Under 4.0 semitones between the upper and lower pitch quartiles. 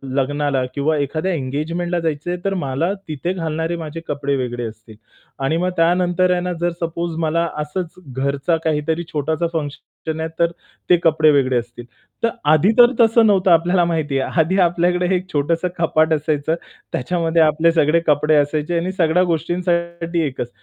Yes: average, 2.9 semitones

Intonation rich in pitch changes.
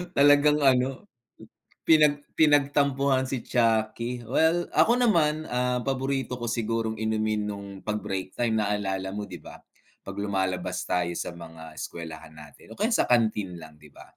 Yes: wide, 6.3 semitones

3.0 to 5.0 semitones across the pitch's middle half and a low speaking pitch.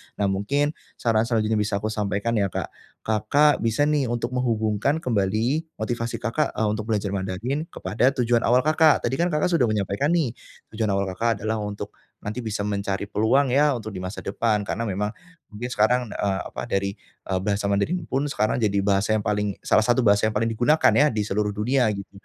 Yes: average, 3.5 semitones; low, 110 Hz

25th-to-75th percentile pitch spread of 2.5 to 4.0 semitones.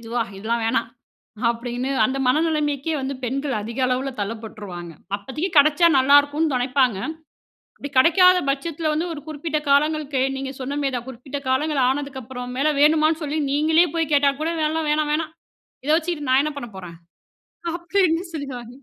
Yes: average, 3.5 semitones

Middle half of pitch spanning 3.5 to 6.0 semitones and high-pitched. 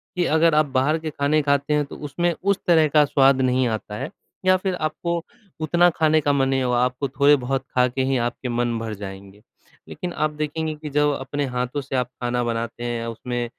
No: average, 3.9 semitones; medium, 140 Hz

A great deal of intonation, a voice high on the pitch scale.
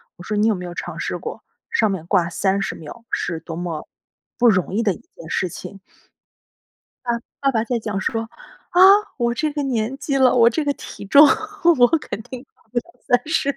Yes: wide, 6.2 semitones; high, 230 Hz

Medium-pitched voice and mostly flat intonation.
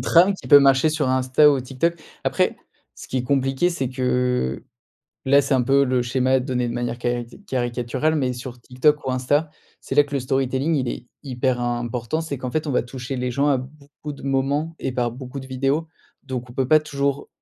No: low, 130 Hz; narrow, 2.3 semitones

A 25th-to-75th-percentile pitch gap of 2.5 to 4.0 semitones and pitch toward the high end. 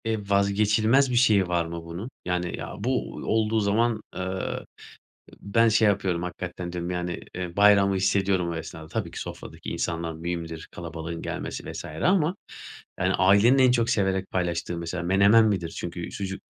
No: average, 3.7 semitones; very low, 95 Hz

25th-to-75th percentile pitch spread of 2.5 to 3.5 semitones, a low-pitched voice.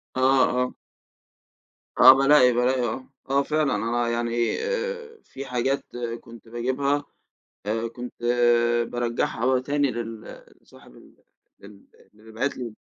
Yes: average, 2.8 semitones; low, 125 Hz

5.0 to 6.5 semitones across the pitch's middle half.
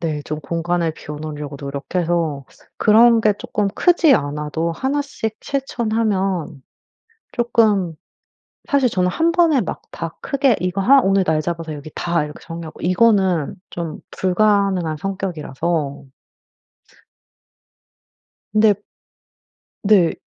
Yes: wide, 5.6 semitones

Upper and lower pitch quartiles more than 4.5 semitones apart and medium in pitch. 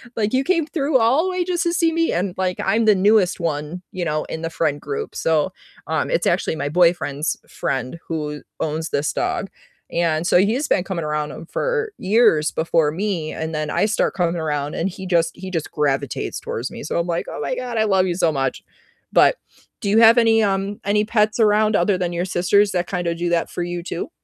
Yes: average, 5.1 semitones; medium, 180 Hz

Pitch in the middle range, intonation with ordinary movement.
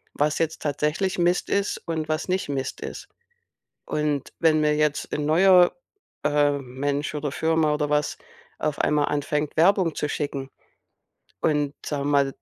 No: medium, 150 Hz; narrow, 1.8 semitones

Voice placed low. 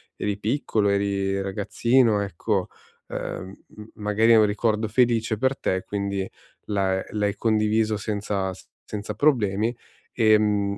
Yes: low, 105 Hz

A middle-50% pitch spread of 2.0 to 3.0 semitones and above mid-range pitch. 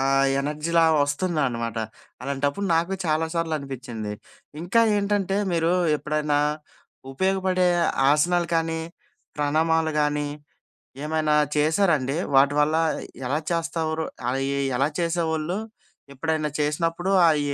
No: average, 2.7 semitones; medium, 155 Hz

